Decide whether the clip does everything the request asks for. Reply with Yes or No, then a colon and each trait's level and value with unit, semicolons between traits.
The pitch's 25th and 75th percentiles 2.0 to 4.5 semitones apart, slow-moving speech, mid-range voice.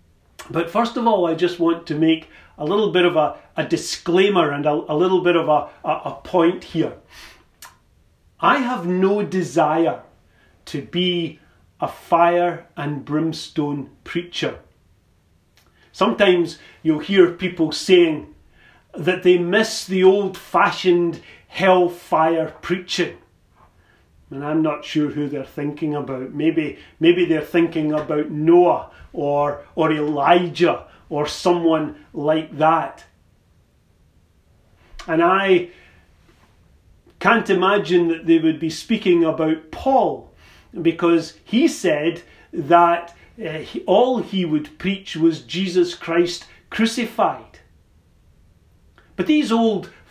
Yes: average, 3.1 semitones; slow, 120 wpm; medium, 165 Hz